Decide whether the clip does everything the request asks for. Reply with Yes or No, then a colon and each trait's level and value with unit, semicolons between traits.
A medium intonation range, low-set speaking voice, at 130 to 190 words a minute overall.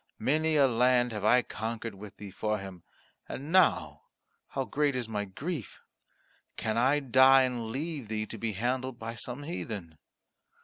Yes: average, 3.8 semitones; low, 120 Hz; average, 165 wpm